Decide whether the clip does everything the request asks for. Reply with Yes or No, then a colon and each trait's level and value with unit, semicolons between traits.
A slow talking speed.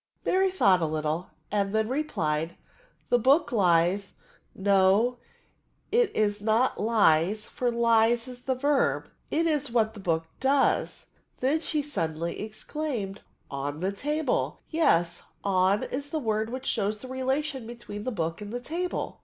No: average, 155 wpm